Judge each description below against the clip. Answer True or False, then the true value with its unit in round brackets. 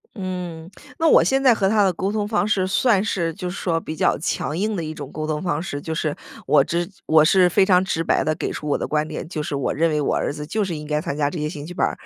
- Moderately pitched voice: True (165 Hz)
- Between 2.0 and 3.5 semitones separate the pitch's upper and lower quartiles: False (3.9 semitones)